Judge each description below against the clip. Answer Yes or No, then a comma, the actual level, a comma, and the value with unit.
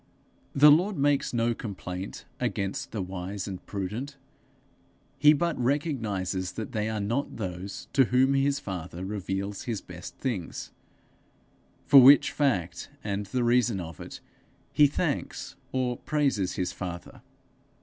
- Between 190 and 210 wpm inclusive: No, slow, 135 wpm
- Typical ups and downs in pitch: No, wide, 6.3 semitones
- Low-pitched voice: Yes, low, 110 Hz